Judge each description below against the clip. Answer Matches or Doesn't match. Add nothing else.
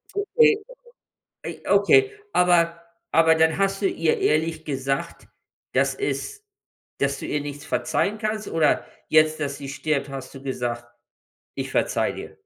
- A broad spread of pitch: Matches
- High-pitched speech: Doesn't match